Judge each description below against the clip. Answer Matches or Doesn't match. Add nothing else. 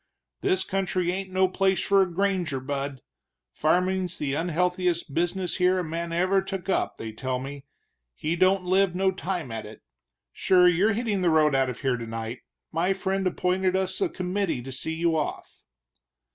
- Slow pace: Doesn't match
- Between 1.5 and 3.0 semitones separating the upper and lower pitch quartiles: Doesn't match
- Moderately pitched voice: Matches